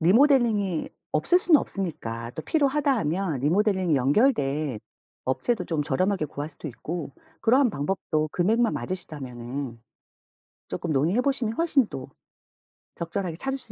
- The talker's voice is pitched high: No, medium, 180 Hz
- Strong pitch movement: Yes, wide, 8.5 semitones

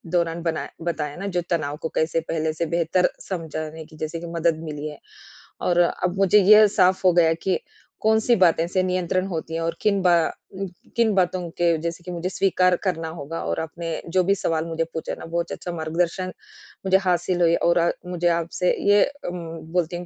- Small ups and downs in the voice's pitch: Yes, narrow, 2.0 semitones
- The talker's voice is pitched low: No, medium, 170 Hz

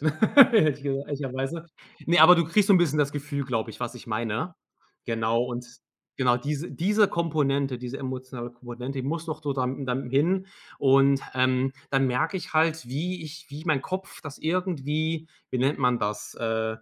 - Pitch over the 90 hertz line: Yes, medium, 140 Hz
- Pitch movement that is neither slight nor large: Yes, average, 4.1 semitones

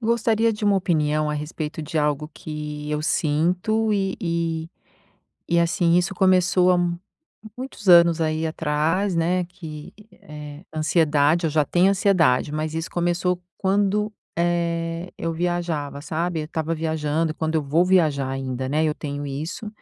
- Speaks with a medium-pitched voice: Yes, medium, 165 Hz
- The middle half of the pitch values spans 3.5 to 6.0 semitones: No, average, 2.9 semitones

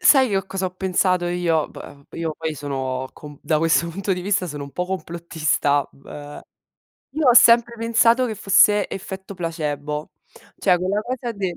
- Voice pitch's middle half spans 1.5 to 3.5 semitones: No, average, 4.8 semitones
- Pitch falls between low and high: Yes, medium, 180 Hz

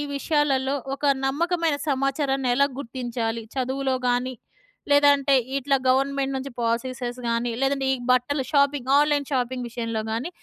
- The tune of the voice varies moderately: No, narrow, 2.2 semitones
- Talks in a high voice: Yes, very high, 270 Hz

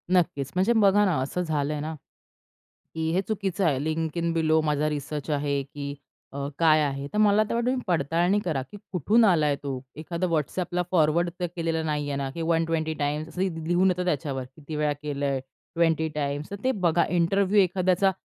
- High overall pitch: No, medium, 160 Hz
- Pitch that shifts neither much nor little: Yes, average, 3.6 semitones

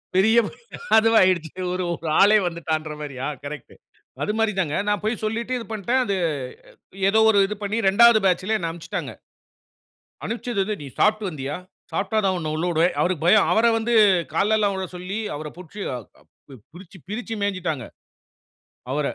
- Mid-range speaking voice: No, high, 195 Hz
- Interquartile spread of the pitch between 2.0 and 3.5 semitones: No, average, 4.6 semitones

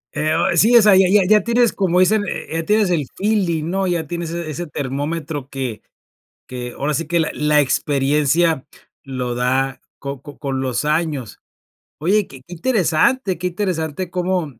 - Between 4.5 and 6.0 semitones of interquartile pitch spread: Yes, average, 4.8 semitones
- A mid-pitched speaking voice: Yes, medium, 160 Hz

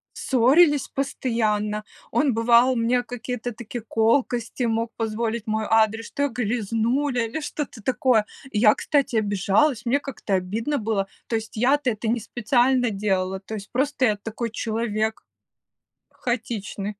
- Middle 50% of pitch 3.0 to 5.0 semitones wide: No, narrow, 2.6 semitones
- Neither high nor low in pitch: No, high, 230 Hz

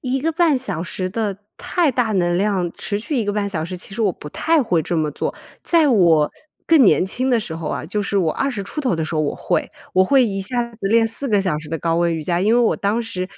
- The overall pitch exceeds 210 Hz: No, high, 200 Hz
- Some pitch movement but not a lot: No, wide, 5.8 semitones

